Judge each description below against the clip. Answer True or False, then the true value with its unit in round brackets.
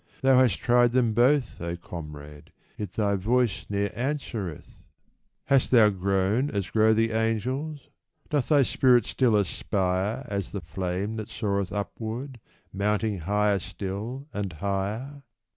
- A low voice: True (105 Hz)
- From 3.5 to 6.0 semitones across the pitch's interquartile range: True (4.1 semitones)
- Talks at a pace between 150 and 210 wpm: False (135 wpm)